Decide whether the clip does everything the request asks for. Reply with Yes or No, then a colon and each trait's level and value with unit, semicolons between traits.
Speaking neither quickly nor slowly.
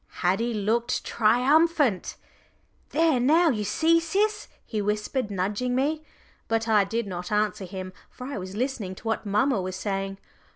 Yes: average, 155 wpm